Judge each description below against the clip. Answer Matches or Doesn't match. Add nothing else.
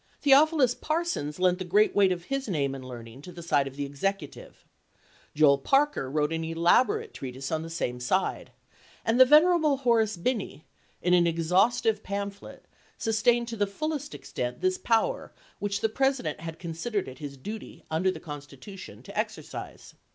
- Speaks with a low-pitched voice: Doesn't match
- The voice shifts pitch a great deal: Matches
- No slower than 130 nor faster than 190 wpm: Matches